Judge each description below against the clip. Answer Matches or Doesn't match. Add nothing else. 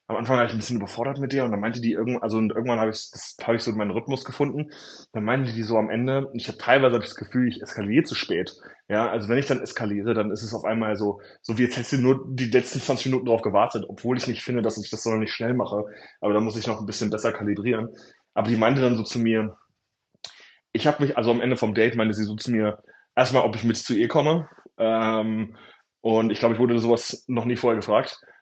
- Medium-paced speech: Doesn't match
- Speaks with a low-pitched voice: Matches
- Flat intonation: Matches